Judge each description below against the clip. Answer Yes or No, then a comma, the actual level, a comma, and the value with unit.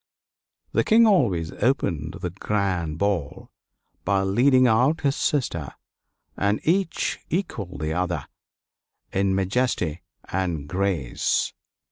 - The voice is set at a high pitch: No, very low, 95 Hz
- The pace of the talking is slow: Yes, slow, 105 wpm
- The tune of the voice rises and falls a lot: Yes, wide, 6.8 semitones